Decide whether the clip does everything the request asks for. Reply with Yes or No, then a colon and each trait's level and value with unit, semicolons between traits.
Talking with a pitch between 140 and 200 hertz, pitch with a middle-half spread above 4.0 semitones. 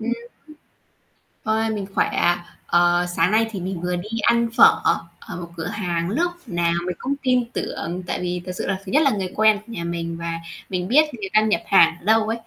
Yes: high, 190 Hz; average, 4.4 semitones